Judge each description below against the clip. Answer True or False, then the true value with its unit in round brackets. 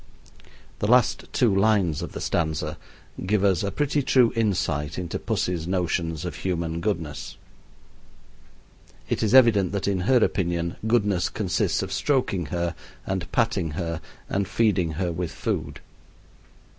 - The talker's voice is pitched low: True (95 Hz)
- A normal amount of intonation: True (4.0 semitones)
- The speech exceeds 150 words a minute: False (140 wpm)